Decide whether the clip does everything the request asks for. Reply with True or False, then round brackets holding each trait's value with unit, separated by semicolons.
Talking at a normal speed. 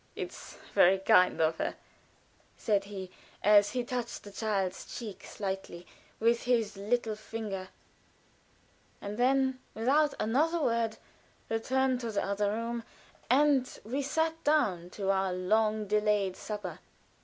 False (130 wpm)